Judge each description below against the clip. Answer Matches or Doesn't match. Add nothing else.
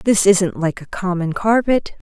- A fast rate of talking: Doesn't match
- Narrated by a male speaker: Doesn't match